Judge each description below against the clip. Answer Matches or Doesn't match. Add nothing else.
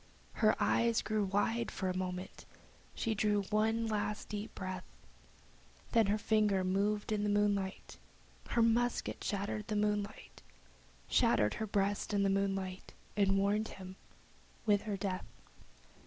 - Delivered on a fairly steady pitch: Matches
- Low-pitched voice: Doesn't match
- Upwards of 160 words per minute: Doesn't match